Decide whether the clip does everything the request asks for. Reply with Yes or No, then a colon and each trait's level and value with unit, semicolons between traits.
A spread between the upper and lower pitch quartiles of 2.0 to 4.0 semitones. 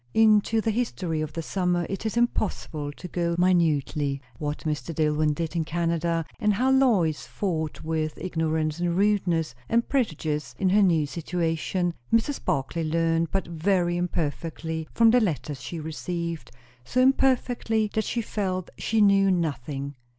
No: average, 4.5 semitones